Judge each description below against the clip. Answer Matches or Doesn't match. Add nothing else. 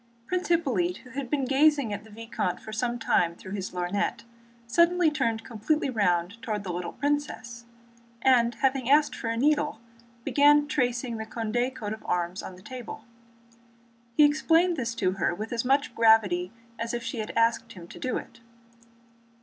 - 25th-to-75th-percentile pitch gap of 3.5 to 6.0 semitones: Matches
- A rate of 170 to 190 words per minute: Matches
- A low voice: Doesn't match